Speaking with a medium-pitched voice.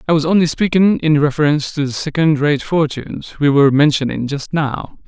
Yes: medium, 150 Hz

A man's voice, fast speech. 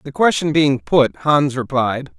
No: male; average, 165 wpm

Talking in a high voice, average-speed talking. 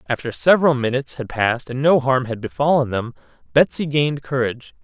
No: low, 130 Hz; average, 175 wpm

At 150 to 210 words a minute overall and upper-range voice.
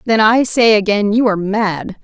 Yes: fast, 205 wpm; high, 215 Hz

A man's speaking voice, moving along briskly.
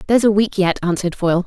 No: female; fast, 245 wpm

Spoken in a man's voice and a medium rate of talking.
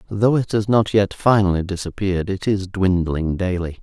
Yes: male; average, 170 wpm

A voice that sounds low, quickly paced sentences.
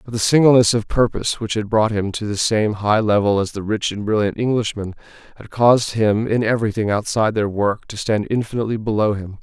Yes: low, 110 Hz; fast, 210 wpm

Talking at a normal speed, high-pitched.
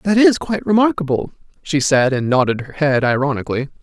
No: average, 175 wpm; medium, 150 Hz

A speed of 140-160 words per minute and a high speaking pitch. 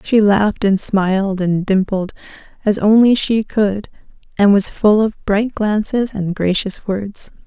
Yes: average, 155 wpm; high, 205 Hz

